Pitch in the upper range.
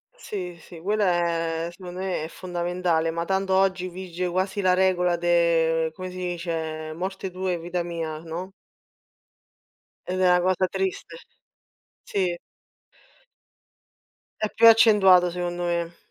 No: medium, 180 Hz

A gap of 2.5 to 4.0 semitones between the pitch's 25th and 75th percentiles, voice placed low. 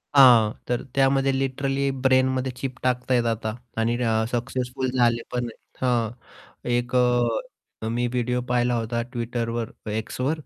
No: narrow, 1.9 semitones; low, 125 Hz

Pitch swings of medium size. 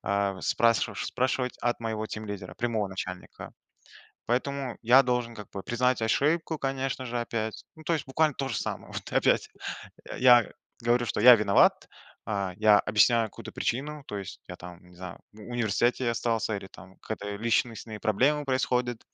Yes: average, 3.3 semitones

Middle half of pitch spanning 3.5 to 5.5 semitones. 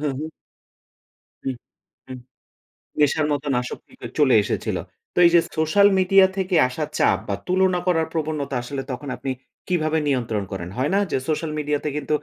Yes: average, 4.0 semitones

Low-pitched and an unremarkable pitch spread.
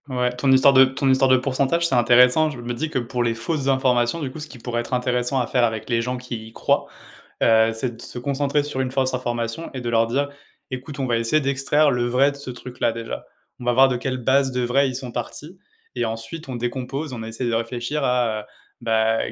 No: low, 125 Hz; narrow, 2.2 semitones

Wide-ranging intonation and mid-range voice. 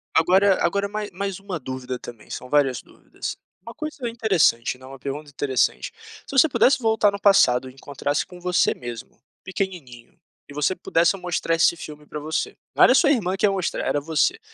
Yes: wide, 6.7 semitones; medium, 170 Hz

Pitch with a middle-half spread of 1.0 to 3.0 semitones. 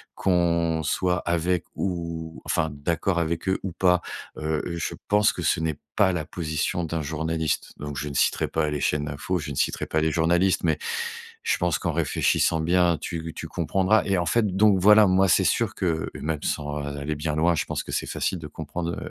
Yes: narrow, 2.5 semitones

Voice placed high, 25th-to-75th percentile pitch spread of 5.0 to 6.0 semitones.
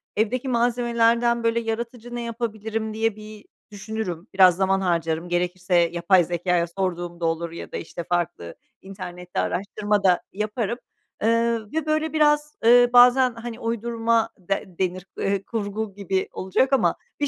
No: high, 215 Hz; average, 4.5 semitones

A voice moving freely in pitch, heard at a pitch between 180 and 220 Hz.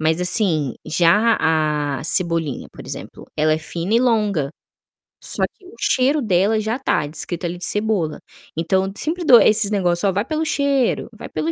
Yes: wide, 6.0 semitones; high, 190 Hz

